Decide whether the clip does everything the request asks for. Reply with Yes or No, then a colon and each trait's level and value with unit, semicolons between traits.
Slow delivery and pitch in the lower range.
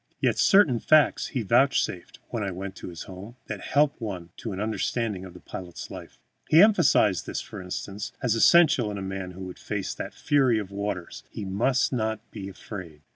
No: average, 195 wpm; low, 105 Hz